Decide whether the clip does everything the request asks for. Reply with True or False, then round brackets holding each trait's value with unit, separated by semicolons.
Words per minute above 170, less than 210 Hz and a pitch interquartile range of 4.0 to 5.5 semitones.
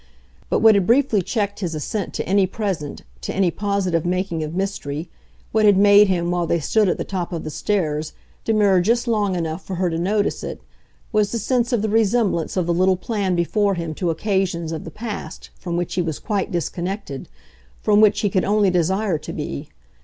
False (205 wpm; 190 Hz; 3.4 semitones)